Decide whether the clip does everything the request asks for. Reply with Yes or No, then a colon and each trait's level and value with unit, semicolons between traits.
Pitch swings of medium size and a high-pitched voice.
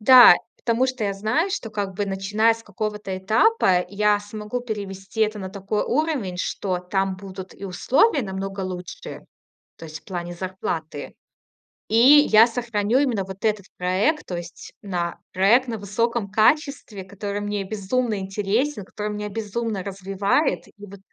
Yes: average, 3.0 semitones; high, 205 Hz